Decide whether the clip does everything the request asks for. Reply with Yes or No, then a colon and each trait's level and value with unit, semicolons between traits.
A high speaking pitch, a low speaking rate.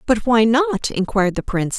No: high, 225 Hz; average, 200 wpm